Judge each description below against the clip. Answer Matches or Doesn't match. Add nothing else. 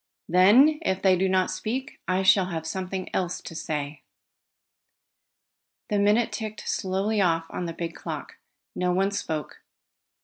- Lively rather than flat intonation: Doesn't match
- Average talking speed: Matches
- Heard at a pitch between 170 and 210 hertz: Matches